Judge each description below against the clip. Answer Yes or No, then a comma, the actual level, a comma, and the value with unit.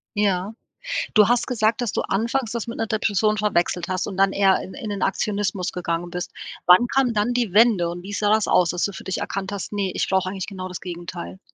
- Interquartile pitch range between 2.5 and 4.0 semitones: Yes, average, 2.8 semitones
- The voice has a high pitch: Yes, high, 200 Hz